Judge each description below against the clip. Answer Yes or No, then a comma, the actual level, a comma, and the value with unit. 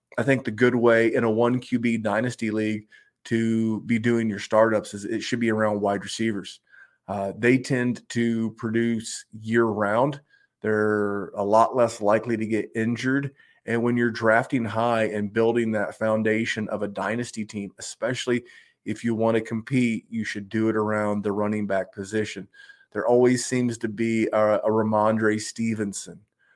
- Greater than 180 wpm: No, average, 170 wpm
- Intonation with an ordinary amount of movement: No, narrow, 1.7 semitones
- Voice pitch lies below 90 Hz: No, low, 110 Hz